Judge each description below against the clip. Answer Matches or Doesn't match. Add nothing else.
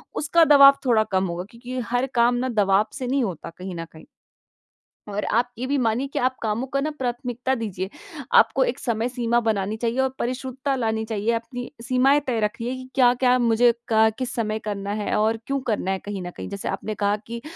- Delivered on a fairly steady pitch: Doesn't match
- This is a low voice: Doesn't match